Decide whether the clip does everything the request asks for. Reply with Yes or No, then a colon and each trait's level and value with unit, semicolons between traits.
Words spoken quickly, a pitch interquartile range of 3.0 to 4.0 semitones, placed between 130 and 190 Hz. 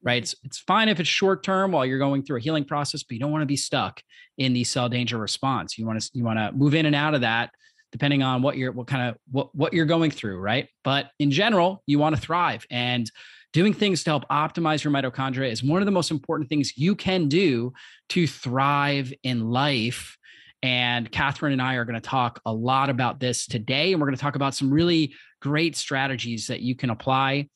Yes: fast, 235 wpm; average, 3.7 semitones; medium, 140 Hz